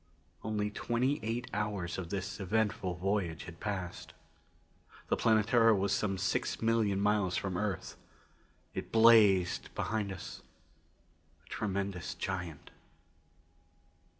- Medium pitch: No, low, 100 Hz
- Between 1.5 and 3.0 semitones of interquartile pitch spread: Yes, average, 2.7 semitones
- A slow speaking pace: Yes, slow, 115 wpm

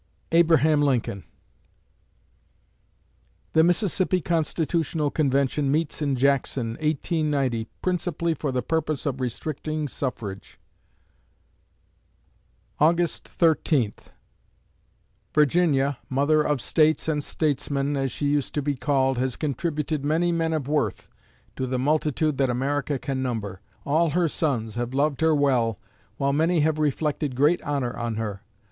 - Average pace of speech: No, slow, 125 wpm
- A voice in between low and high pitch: Yes, medium, 145 Hz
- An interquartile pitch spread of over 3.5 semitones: No, average, 3.1 semitones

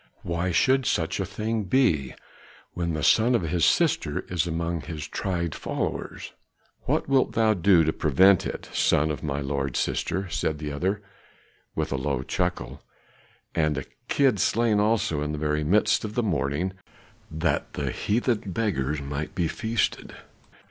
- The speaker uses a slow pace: No, average, 160 wpm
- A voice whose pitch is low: Yes, very low, 85 Hz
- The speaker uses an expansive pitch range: Yes, wide, 5.8 semitones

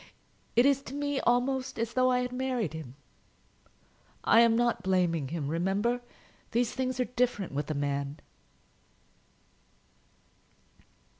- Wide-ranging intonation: Yes, wide, 7.3 semitones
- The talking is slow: Yes, slow, 130 wpm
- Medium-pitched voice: No, high, 235 Hz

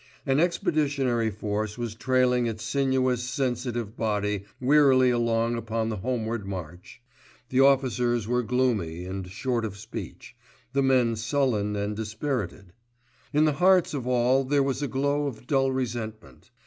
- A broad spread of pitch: No, average, 3.5 semitones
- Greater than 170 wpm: No, average, 145 wpm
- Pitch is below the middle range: Yes, low, 120 Hz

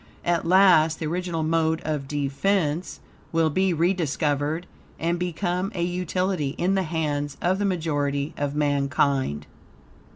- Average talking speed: No, slow, 130 wpm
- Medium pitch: Yes, medium, 160 Hz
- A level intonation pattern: No, average, 3.5 semitones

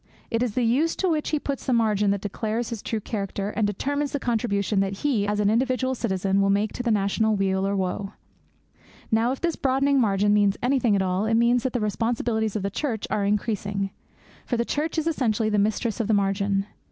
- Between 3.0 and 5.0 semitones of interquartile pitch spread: Yes, average, 3.6 semitones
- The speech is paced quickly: Yes, fast, 220 wpm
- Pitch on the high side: Yes, high, 220 Hz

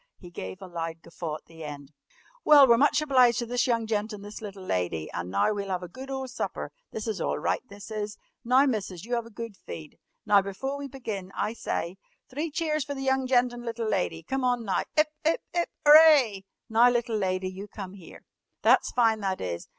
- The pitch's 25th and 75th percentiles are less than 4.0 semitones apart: No, wide, 5.6 semitones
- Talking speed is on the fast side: Yes, fast, 220 wpm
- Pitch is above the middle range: Yes, high, 220 Hz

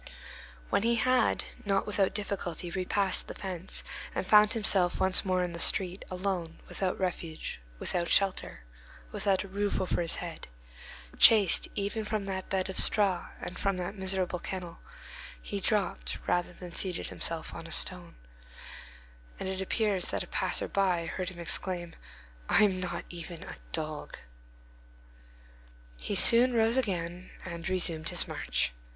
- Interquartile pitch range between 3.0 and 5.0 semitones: No, narrow, 2.4 semitones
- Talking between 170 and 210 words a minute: No, average, 150 wpm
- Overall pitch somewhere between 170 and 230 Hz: Yes, medium, 185 Hz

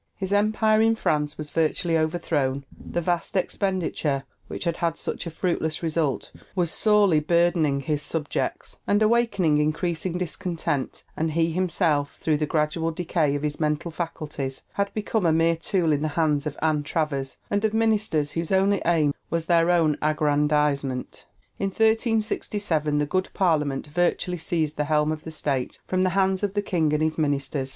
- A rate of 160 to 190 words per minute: Yes, average, 170 wpm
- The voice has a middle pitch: Yes, medium, 160 Hz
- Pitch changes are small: No, average, 3.6 semitones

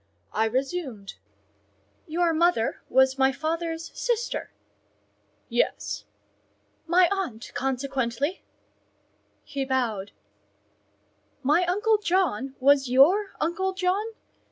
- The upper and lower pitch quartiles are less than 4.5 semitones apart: No, wide, 5.6 semitones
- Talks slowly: Yes, slow, 85 wpm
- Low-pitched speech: No, very high, 305 Hz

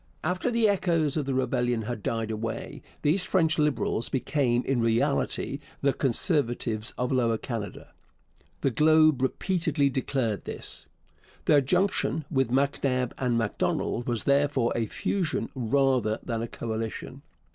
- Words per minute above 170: No, slow, 135 wpm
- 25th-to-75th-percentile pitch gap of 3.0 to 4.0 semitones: No, average, 4.4 semitones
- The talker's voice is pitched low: Yes, low, 130 Hz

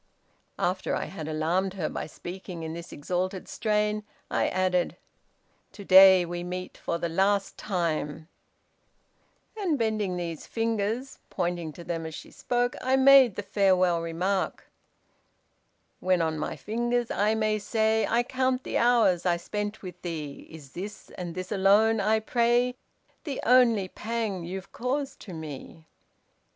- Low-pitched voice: No, high, 190 Hz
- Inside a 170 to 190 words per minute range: No, average, 145 wpm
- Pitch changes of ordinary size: Yes, average, 4.4 semitones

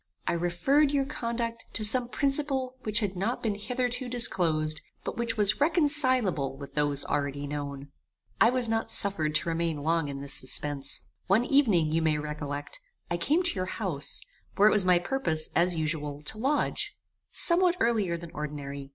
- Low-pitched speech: No, medium, 185 Hz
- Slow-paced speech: No, average, 170 wpm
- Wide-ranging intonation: Yes, wide, 8.4 semitones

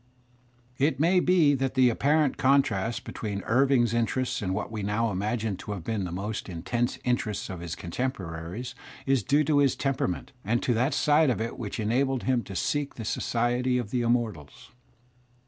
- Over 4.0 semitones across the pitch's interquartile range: Yes, average, 4.5 semitones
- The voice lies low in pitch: Yes, low, 120 Hz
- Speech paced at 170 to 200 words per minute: Yes, average, 180 wpm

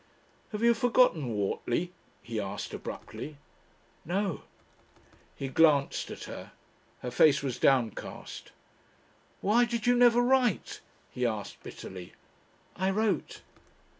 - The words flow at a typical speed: No, slow, 110 wpm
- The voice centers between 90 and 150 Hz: No, medium, 165 Hz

